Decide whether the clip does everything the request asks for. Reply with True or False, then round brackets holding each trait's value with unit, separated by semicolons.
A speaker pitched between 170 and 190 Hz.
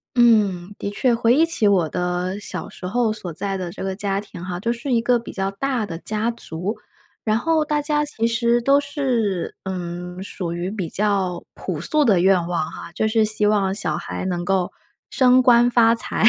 False (205 Hz)